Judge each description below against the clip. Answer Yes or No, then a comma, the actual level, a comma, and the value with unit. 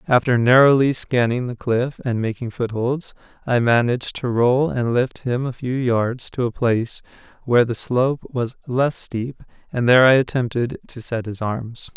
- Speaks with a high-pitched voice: No, low, 125 Hz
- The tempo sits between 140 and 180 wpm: Yes, average, 175 wpm